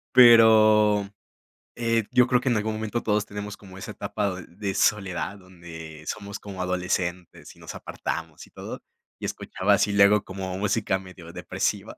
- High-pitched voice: No, low, 100 Hz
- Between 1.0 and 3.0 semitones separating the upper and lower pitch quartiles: Yes, average, 2.7 semitones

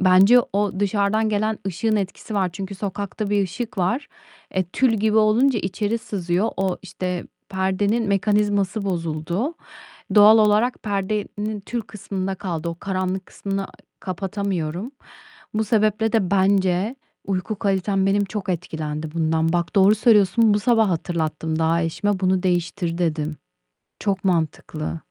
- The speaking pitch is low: No, high, 195 Hz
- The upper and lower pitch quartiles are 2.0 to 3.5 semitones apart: Yes, average, 2.8 semitones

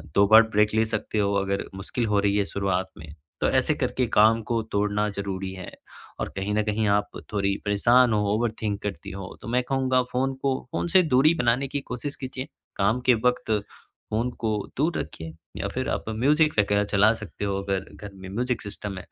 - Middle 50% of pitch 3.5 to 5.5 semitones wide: Yes, average, 3.9 semitones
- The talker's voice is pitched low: Yes, low, 105 Hz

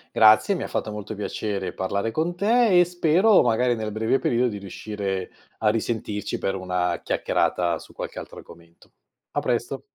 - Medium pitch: No, low, 110 Hz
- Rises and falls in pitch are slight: No, wide, 5.4 semitones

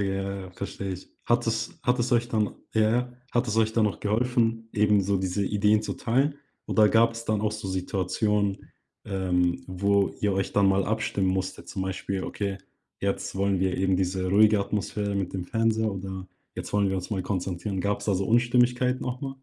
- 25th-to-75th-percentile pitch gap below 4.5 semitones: Yes, average, 2.8 semitones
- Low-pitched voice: Yes, low, 100 Hz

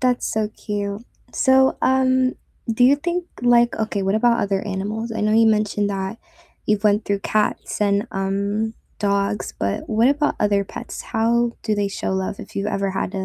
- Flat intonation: No, average, 3.0 semitones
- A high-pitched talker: Yes, high, 215 Hz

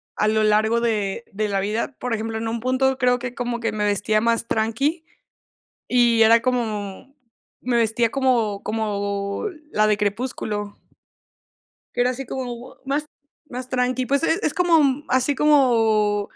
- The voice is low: No, high, 235 Hz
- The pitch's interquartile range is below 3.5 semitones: Yes, average, 3.1 semitones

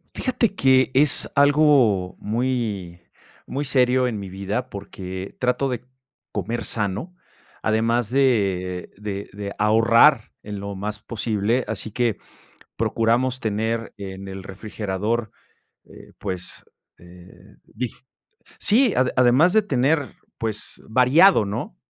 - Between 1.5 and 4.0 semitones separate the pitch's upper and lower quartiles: No, average, 4.4 semitones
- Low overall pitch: Yes, low, 115 Hz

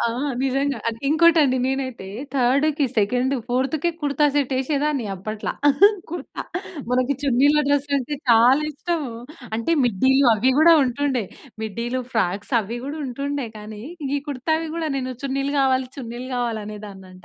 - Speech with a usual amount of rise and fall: Yes, average, 3.5 semitones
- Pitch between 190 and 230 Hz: No, very high, 260 Hz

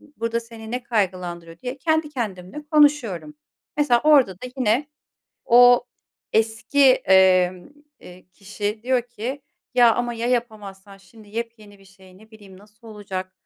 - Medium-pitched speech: No, high, 220 Hz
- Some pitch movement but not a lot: Yes, average, 4.1 semitones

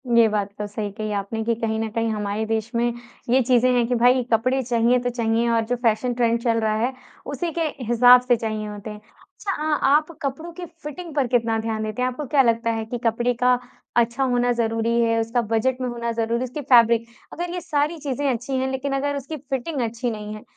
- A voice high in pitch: Yes, high, 240 Hz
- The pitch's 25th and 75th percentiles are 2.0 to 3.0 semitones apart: Yes, average, 2.7 semitones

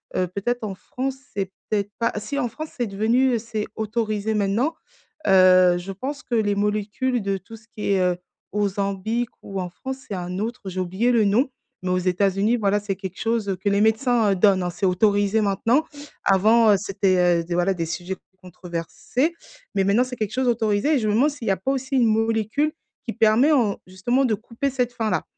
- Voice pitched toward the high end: Yes, high, 210 Hz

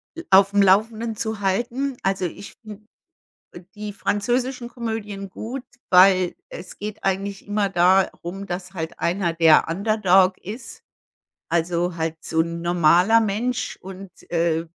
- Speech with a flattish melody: No, average, 3.4 semitones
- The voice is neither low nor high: No, high, 195 Hz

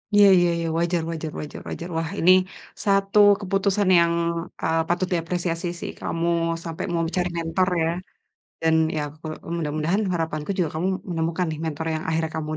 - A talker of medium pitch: Yes, medium, 165 Hz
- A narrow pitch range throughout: Yes, narrow, 2.0 semitones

